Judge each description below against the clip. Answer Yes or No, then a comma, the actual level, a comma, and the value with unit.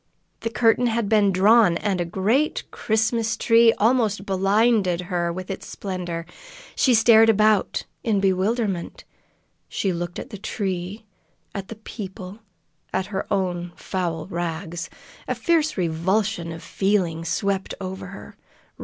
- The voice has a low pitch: No, high, 195 Hz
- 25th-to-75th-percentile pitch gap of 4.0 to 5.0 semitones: No, average, 3.6 semitones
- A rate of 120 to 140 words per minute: Yes, slow, 135 wpm